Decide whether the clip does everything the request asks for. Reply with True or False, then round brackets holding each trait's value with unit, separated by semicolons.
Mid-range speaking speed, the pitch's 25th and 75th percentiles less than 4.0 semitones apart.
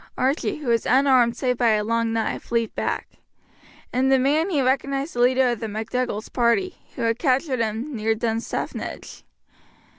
True (170 wpm; 2.8 semitones)